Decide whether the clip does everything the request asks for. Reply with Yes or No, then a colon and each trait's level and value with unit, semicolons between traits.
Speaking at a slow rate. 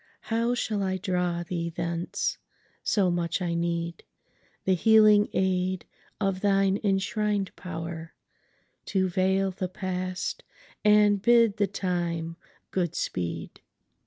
Yes: slow, 100 wpm